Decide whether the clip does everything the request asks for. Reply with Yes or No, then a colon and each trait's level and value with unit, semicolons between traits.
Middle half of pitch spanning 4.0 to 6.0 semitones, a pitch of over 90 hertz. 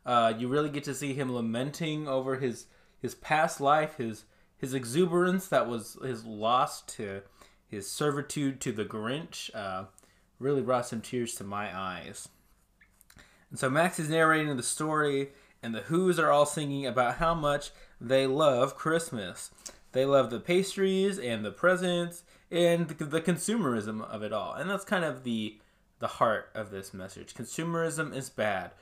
Yes: wide, 5.5 semitones; medium, 140 Hz